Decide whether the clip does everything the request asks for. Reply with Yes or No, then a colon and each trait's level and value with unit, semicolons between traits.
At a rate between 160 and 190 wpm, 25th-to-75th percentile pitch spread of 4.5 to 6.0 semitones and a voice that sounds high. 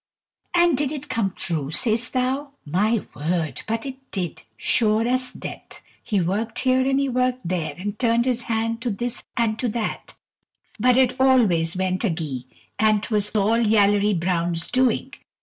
Yes: average, 165 wpm; average, 5.2 semitones; high, 225 Hz